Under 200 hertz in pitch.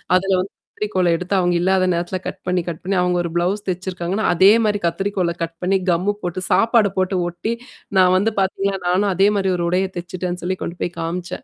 Yes: medium, 185 Hz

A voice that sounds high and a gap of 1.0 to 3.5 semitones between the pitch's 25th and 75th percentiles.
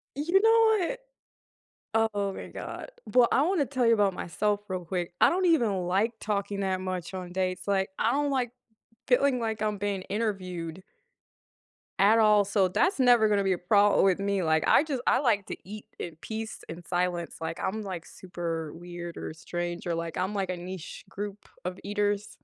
No: high, 200 Hz; average, 3.9 semitones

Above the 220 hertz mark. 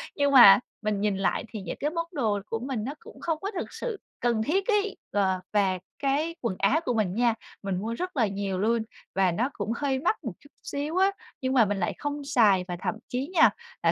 Yes: high, 240 Hz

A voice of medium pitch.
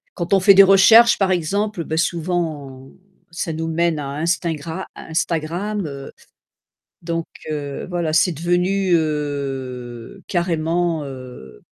Yes: medium, 165 Hz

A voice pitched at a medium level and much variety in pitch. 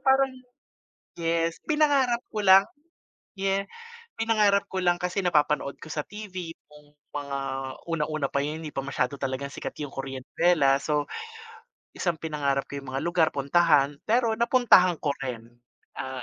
Yes: medium, 165 Hz; wide, 5.8 semitones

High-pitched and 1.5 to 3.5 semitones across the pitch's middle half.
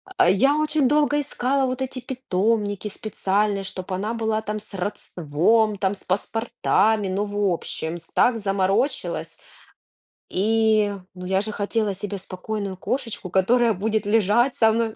Yes: high, 210 Hz; average, 3.0 semitones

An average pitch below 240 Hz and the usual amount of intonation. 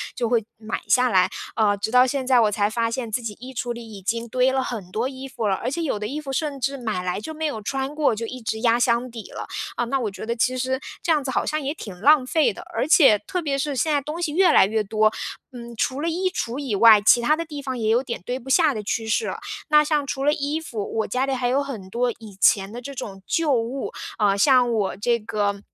No: high, 245 Hz; average, 4.0 semitones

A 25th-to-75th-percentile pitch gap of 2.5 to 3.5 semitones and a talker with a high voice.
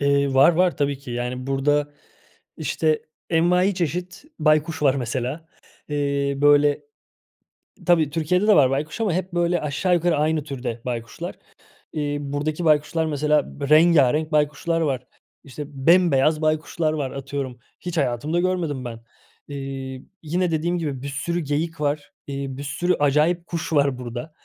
No: average, 3.1 semitones; medium, 150 Hz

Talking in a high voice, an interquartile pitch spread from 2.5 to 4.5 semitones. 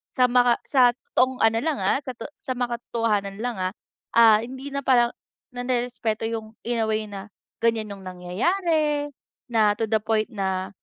Yes: high, 230 Hz; average, 2.9 semitones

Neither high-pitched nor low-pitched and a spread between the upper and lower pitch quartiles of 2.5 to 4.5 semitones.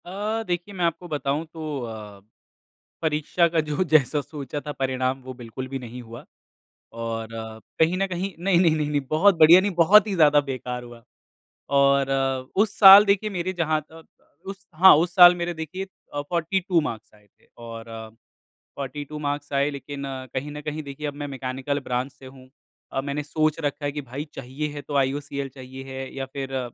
Yes: medium, 145 Hz; average, 4.2 semitones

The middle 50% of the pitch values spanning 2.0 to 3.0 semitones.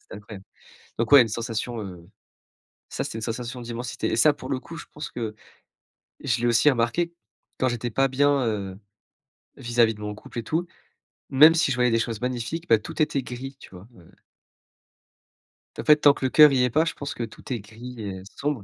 No: average, 3.7 semitones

